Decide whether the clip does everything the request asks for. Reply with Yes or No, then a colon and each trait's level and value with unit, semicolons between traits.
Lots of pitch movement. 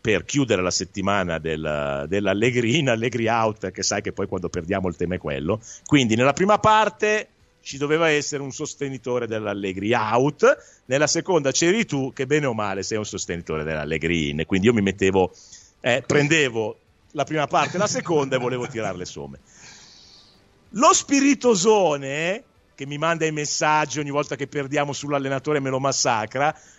Yes: wide, 7.5 semitones